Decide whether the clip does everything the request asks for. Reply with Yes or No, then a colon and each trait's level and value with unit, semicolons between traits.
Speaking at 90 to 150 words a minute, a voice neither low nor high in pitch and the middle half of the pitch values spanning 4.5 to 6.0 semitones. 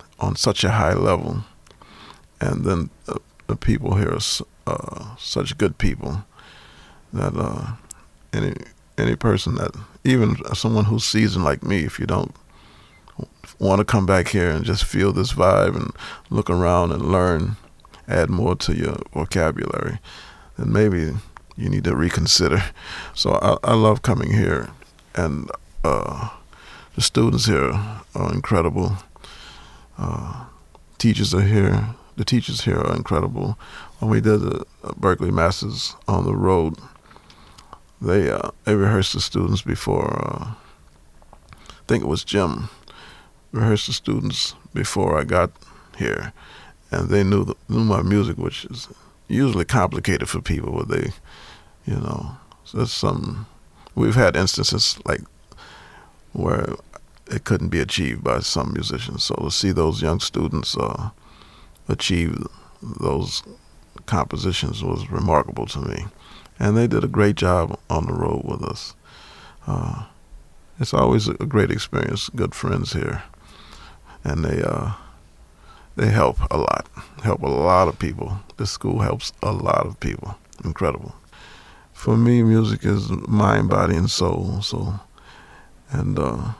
No: average, 140 wpm; low, 100 Hz; average, 4.8 semitones